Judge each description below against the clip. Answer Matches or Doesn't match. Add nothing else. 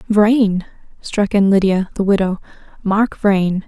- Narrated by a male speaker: Doesn't match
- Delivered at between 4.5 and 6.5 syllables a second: Doesn't match